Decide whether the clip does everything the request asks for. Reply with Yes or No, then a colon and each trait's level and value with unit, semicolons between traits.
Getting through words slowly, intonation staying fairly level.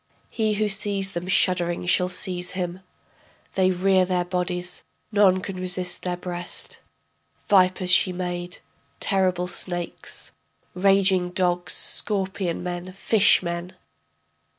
Yes: slow, 115 wpm; narrow, 1.3 semitones